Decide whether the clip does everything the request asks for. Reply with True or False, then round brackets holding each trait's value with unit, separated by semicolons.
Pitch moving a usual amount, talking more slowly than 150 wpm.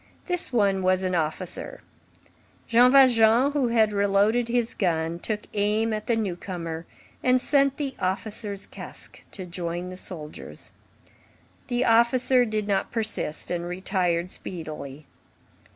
True (4.8 semitones; 135 wpm)